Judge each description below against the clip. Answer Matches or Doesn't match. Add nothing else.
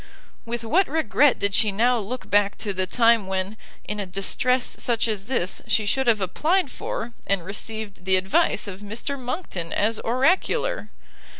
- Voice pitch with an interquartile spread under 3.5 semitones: Doesn't match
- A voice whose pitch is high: Matches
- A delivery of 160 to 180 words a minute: Matches